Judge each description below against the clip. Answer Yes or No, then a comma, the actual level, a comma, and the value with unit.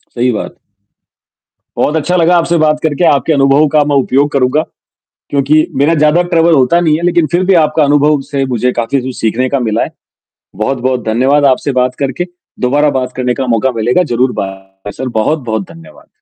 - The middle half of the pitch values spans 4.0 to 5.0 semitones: No, average, 3.5 semitones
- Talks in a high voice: No, medium, 140 Hz